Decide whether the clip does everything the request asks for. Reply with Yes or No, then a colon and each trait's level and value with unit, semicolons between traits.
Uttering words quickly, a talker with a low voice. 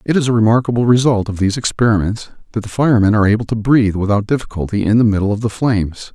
Yes: fast, 225 wpm; low, 110 Hz